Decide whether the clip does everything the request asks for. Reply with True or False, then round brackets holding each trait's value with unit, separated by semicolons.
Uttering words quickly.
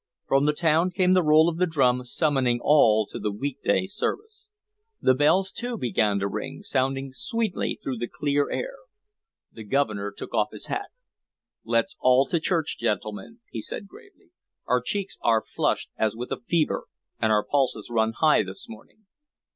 False (175 wpm)